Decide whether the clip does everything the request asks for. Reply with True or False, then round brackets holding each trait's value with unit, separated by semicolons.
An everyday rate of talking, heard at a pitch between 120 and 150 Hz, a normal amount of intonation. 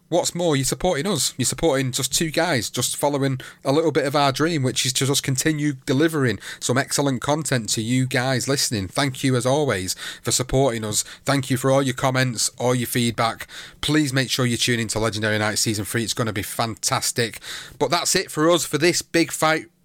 False (220 wpm; 135 Hz; 3.6 semitones)